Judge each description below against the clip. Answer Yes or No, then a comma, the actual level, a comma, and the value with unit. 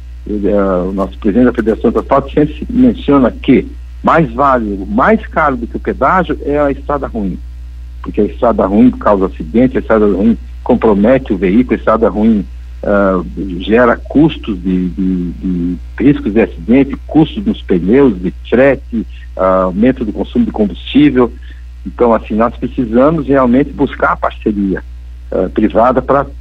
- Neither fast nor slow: Yes, average, 155 wpm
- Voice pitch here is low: Yes, low, 100 Hz